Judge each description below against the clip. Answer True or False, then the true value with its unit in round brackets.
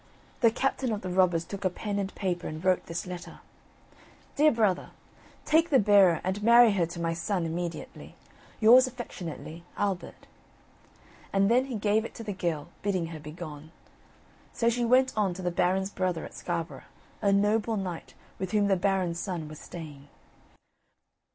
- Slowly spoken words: False (170 wpm)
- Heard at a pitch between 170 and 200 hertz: True (190 Hz)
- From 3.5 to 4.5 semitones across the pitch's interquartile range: True (3.9 semitones)